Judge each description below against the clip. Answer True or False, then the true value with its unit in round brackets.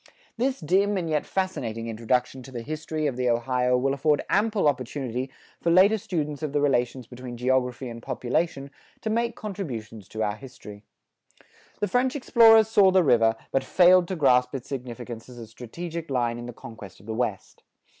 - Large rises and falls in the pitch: True (6.5 semitones)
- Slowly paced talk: False (180 wpm)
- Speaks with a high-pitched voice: False (135 Hz)